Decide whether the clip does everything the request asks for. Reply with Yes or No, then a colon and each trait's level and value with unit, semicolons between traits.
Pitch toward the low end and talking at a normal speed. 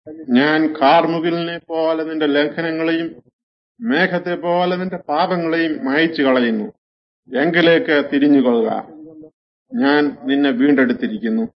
No: medium, 160 Hz; average, 85 wpm